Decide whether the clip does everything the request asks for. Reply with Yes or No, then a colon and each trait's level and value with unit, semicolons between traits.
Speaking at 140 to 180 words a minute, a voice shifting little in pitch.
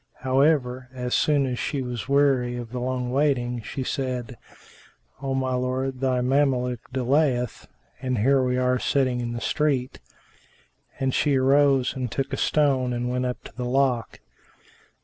Yes: average, 155 wpm; narrow, 1.6 semitones